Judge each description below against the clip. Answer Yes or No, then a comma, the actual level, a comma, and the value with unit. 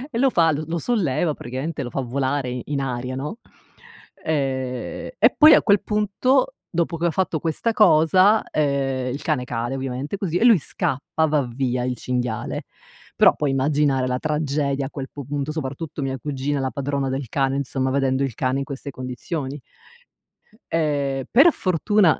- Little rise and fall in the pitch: No, average, 3.6 semitones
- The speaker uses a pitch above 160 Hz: No, medium, 140 Hz